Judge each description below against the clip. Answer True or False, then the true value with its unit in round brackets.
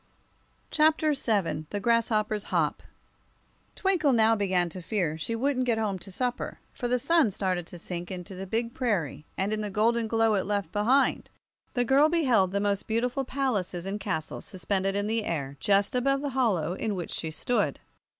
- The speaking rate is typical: True (180 wpm)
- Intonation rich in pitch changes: False (4.7 semitones)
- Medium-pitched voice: False (210 Hz)